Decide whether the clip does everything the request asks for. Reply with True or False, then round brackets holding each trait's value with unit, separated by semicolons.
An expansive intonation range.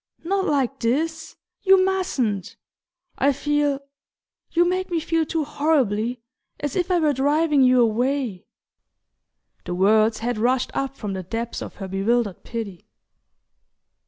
True (5.9 semitones)